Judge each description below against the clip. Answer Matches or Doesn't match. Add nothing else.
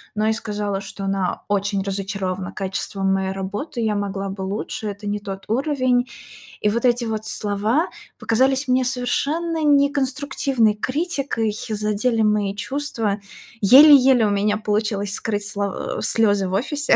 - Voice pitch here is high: Matches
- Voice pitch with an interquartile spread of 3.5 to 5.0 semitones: Matches